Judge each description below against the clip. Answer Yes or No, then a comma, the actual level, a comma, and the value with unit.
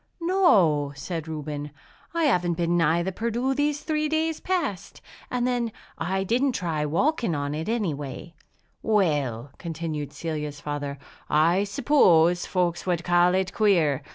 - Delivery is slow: No, average, 145 wpm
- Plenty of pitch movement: Yes, wide, 7.6 semitones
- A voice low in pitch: No, medium, 175 Hz